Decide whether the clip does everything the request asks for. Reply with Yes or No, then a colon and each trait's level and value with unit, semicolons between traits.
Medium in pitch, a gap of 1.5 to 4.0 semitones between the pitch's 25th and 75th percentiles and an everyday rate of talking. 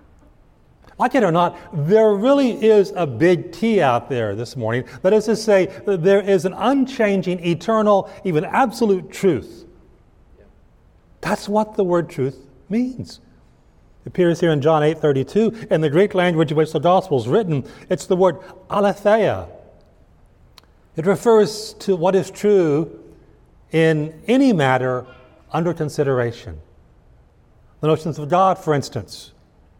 No: medium, 180 Hz; wide, 5.4 semitones; average, 145 wpm